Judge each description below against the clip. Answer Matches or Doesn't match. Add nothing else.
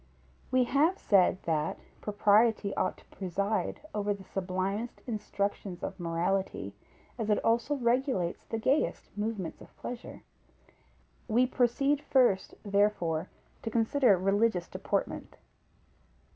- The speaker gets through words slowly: Matches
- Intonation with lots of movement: Doesn't match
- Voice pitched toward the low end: Doesn't match